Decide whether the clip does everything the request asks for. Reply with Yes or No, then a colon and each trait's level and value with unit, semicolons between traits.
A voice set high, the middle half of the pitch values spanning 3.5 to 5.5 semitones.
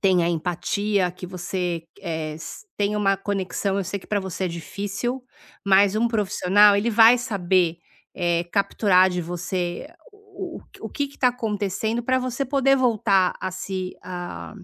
No: high, 195 Hz; average, 3.1 semitones